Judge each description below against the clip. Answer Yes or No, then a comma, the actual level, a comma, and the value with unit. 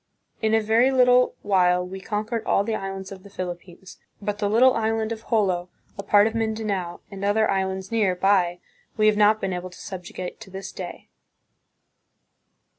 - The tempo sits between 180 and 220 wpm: Yes, average, 190 wpm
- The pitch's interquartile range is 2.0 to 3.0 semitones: Yes, average, 2.7 semitones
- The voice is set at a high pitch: Yes, high, 200 Hz